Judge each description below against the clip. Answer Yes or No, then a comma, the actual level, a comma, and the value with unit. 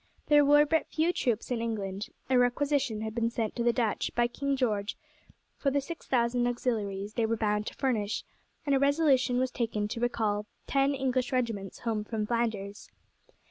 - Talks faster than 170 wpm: Yes, average, 180 wpm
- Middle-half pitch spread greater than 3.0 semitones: Yes, average, 3.8 semitones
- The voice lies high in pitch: Yes, high, 240 Hz